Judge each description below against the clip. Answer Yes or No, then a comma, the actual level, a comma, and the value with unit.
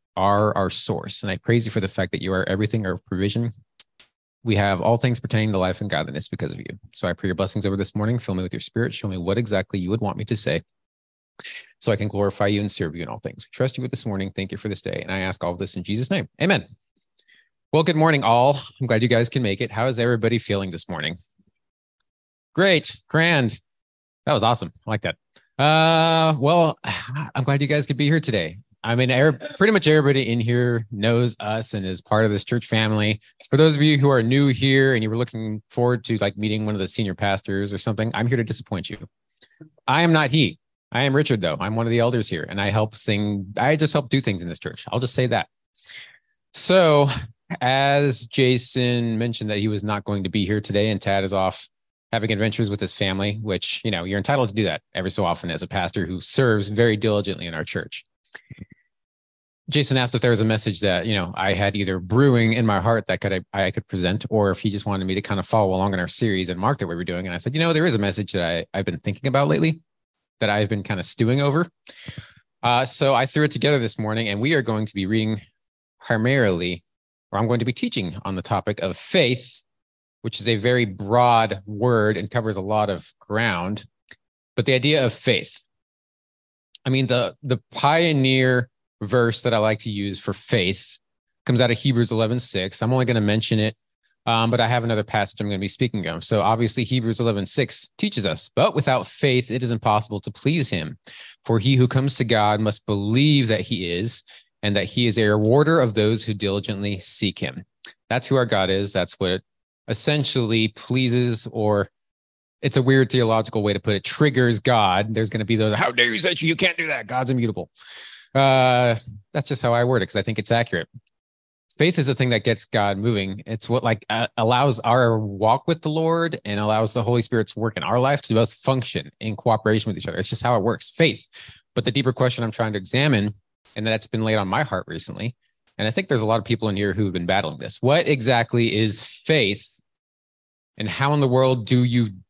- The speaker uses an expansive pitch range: No, average, 3.9 semitones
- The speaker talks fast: Yes, fast, 230 wpm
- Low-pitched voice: Yes, low, 110 Hz